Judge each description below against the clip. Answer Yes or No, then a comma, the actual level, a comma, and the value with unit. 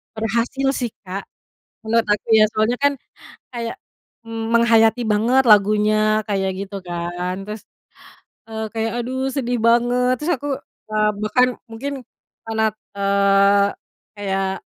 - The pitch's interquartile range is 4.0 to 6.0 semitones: No, average, 2.9 semitones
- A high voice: Yes, high, 220 Hz